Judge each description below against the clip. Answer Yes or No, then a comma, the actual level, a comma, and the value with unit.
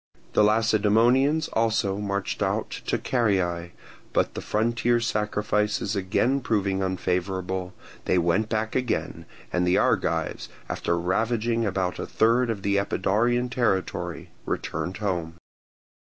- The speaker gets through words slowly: Yes, slow, 120 wpm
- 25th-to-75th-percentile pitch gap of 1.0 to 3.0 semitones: No, average, 3.5 semitones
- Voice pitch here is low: Yes, low, 105 Hz